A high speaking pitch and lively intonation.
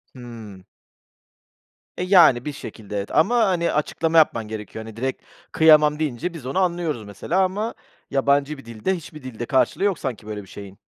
No: medium, 140 Hz; wide, 7.1 semitones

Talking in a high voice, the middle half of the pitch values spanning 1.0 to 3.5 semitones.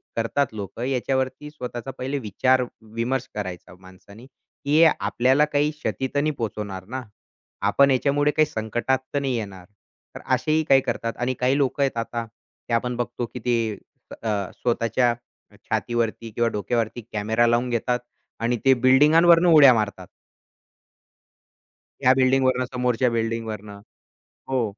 No: low, 125 Hz; average, 2.8 semitones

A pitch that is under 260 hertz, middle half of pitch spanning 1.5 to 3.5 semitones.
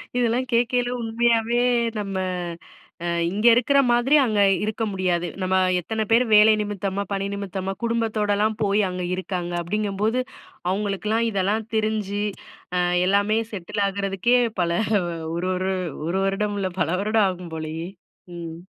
Yes: high, 205 Hz; average, 2.9 semitones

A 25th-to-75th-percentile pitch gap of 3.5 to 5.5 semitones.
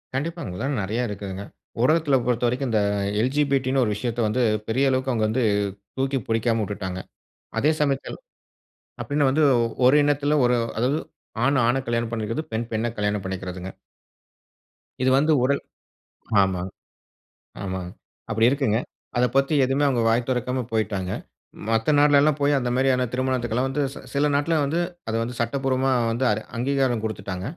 Yes: average, 3.8 semitones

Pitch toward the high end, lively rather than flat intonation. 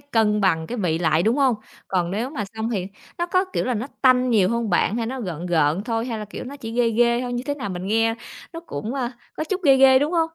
No: high, 230 Hz; average, 4.6 semitones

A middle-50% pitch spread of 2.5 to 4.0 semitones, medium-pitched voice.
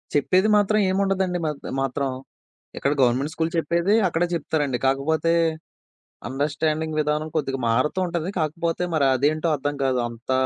Yes: average, 3.6 semitones; medium, 155 Hz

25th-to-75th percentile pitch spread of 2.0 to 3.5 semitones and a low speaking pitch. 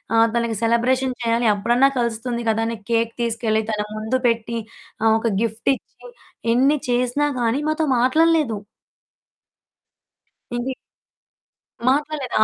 No: narrow, 2.5 semitones; high, 235 Hz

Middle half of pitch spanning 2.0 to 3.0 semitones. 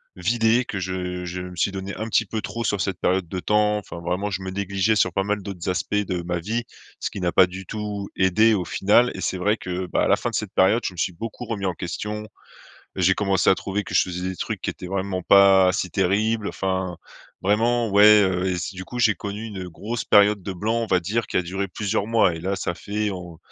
Yes: narrow, 2.5 semitones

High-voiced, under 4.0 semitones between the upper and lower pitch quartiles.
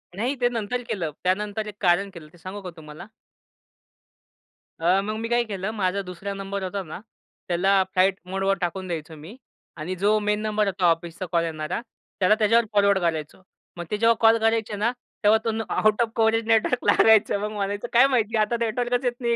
Yes: high, 205 Hz; average, 3.4 semitones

